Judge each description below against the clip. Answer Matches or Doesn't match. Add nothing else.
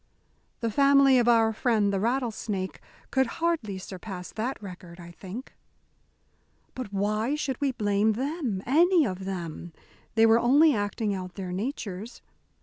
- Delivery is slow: Doesn't match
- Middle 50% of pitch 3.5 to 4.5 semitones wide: Doesn't match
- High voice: Matches